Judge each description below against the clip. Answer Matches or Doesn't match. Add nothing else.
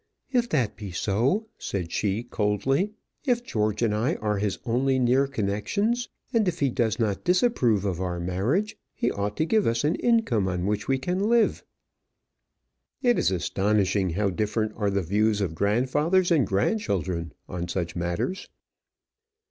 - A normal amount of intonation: Doesn't match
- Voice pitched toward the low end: Matches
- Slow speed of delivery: Doesn't match